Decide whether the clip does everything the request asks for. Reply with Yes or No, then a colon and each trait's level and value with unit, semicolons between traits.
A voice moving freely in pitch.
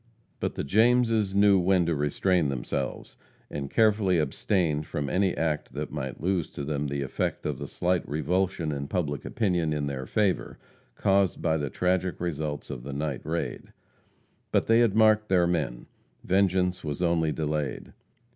No: average, 4.7 semitones